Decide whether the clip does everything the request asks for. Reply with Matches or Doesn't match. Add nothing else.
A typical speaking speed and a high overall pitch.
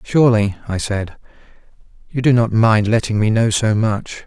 Doesn't match